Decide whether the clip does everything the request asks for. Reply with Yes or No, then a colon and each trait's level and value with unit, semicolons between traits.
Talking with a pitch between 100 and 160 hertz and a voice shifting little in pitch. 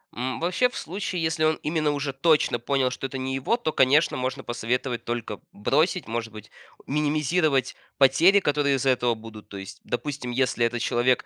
No: low, 135 Hz; average, 4.3 semitones